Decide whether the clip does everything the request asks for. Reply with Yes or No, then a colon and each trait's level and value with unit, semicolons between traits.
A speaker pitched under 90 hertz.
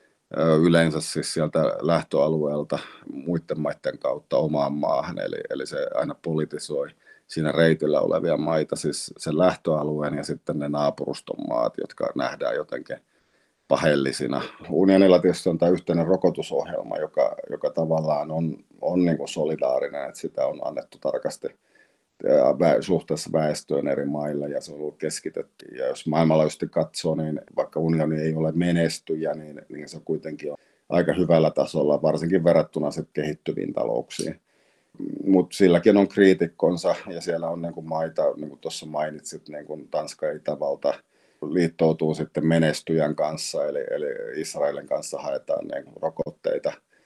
Yes: very low, 80 Hz